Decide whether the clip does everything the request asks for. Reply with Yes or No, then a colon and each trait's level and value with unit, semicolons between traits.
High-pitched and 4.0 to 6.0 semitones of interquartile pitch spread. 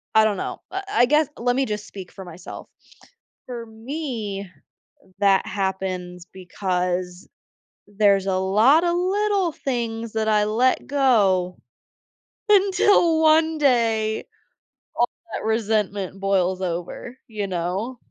Yes: high, 215 Hz; wide, 5.4 semitones